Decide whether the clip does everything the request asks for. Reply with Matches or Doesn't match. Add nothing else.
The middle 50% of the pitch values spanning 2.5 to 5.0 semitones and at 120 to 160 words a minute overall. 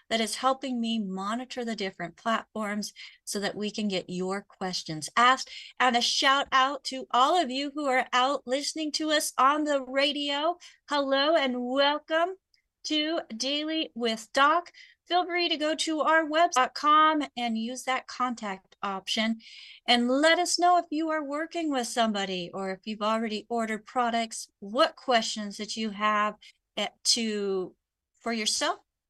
Doesn't match